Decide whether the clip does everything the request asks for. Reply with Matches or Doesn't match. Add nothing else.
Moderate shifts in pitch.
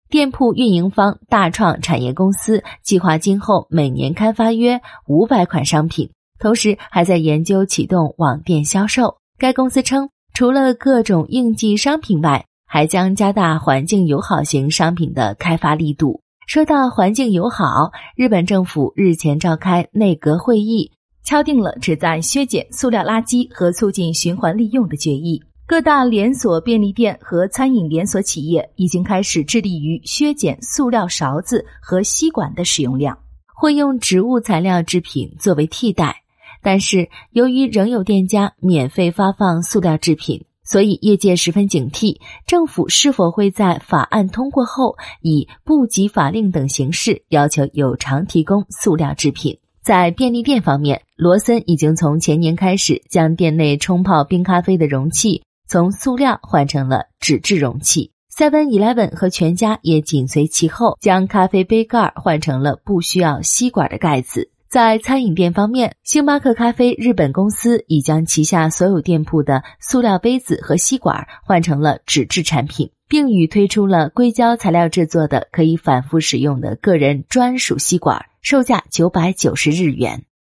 Doesn't match